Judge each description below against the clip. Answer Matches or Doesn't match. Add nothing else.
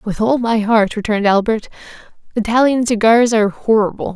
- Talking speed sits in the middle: Matches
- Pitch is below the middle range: Doesn't match